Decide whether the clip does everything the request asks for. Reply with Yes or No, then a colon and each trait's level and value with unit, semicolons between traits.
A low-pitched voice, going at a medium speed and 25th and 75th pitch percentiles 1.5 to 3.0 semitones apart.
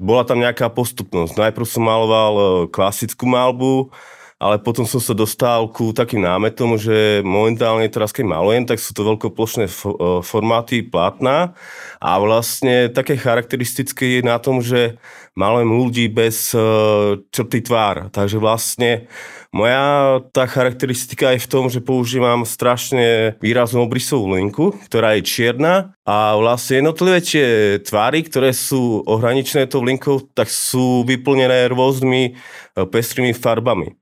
Yes: low, 120 Hz; average, 130 wpm; average, 2.7 semitones